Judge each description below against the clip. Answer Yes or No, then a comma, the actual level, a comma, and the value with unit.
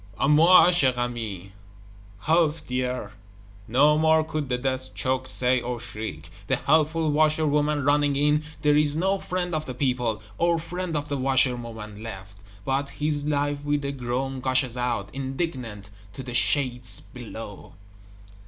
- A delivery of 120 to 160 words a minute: Yes, average, 155 wpm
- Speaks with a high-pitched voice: No, low, 135 Hz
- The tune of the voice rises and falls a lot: No, average, 3.6 semitones